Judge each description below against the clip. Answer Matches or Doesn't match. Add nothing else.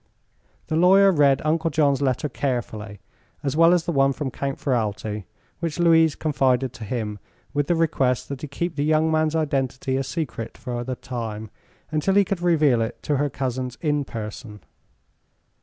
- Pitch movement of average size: Matches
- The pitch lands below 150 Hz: Matches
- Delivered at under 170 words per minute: Doesn't match